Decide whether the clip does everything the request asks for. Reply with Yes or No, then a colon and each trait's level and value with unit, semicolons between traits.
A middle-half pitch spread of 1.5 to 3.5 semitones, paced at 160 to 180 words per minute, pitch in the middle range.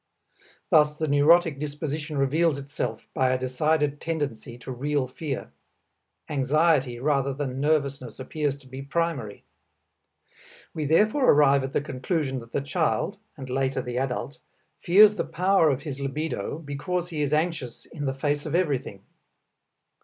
No: average, 2.9 semitones; average, 145 wpm; medium, 145 Hz